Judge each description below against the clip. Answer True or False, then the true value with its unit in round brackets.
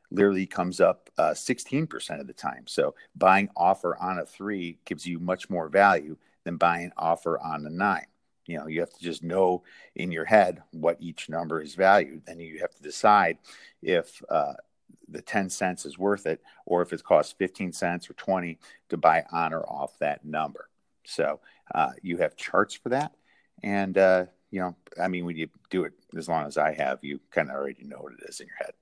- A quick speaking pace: True (210 wpm)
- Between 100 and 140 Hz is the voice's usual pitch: False (90 Hz)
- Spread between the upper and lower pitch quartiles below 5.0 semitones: True (2.5 semitones)